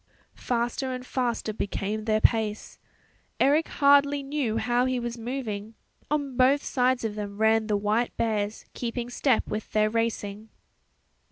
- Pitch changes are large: No, average, 3.1 semitones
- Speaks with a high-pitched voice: Yes, high, 230 Hz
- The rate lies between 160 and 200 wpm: No, average, 145 wpm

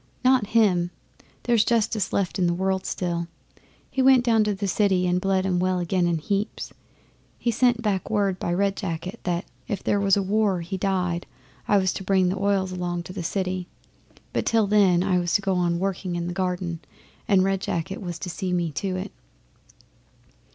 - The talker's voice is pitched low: No, high, 190 Hz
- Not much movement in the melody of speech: Yes, narrow, 2.2 semitones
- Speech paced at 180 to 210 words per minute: Yes, average, 200 wpm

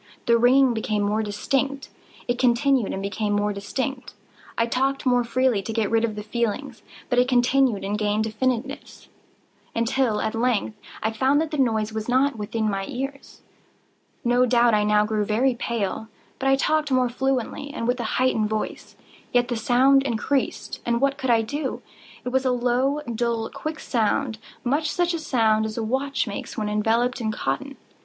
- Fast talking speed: No, average, 170 wpm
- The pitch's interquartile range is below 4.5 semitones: Yes, average, 3.5 semitones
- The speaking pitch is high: Yes, high, 240 Hz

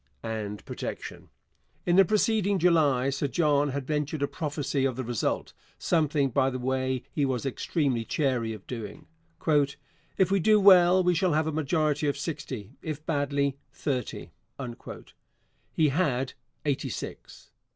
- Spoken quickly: No, average, 145 wpm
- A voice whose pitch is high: No, medium, 145 Hz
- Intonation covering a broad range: No, average, 3.5 semitones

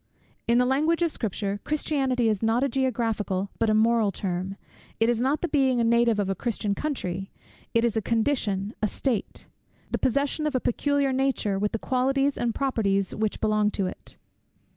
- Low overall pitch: No, high, 230 Hz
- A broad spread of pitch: No, average, 4.3 semitones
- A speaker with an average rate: Yes, average, 185 wpm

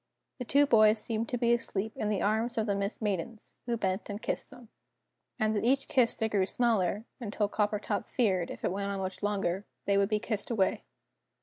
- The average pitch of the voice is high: Yes, high, 215 Hz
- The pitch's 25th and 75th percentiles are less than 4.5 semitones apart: Yes, narrow, 2.5 semitones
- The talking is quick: Yes, fast, 210 wpm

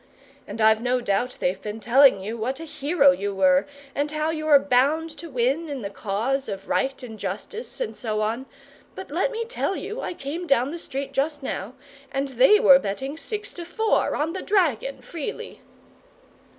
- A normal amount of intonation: No, wide, 5.9 semitones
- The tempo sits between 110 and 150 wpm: No, average, 190 wpm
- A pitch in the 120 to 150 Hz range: No, very high, 275 Hz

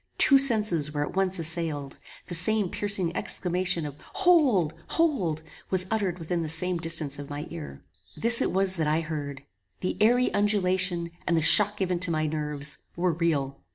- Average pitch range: Yes, average, 3.9 semitones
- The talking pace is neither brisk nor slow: Yes, average, 175 wpm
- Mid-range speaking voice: Yes, medium, 175 Hz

